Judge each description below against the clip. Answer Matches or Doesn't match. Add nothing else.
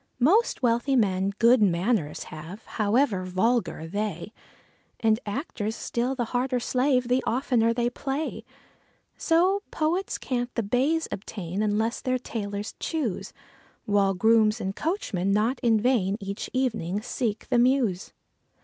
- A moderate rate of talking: Doesn't match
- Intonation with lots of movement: Doesn't match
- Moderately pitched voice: Doesn't match